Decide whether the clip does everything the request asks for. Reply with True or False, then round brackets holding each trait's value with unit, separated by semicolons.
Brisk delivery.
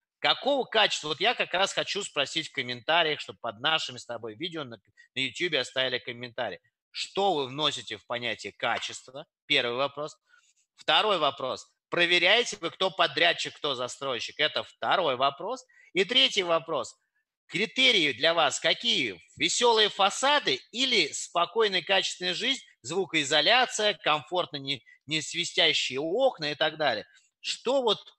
False (135 wpm)